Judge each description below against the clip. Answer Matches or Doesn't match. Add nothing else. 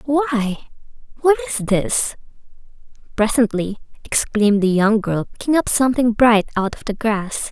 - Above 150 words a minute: Doesn't match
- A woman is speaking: Matches